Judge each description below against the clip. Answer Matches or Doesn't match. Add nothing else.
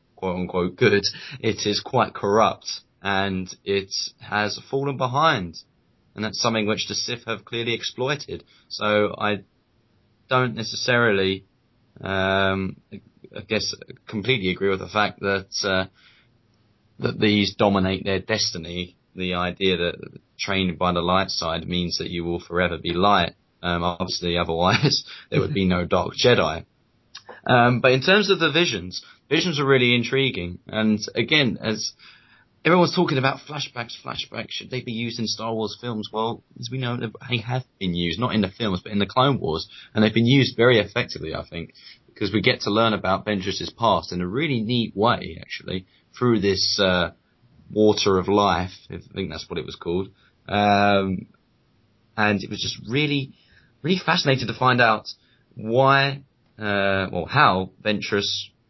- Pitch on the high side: Doesn't match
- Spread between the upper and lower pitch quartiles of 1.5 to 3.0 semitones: Doesn't match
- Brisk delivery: Doesn't match